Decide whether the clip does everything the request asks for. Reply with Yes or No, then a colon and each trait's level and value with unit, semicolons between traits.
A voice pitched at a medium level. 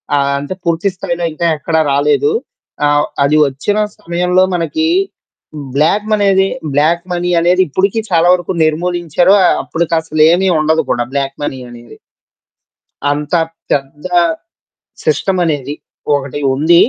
Yes: medium, 165 Hz